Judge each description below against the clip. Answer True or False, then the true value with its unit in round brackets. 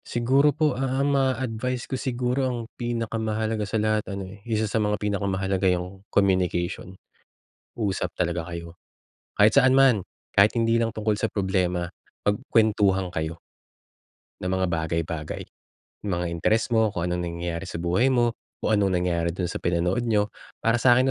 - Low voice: True (105 Hz)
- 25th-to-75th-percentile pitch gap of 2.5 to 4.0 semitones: False (4.6 semitones)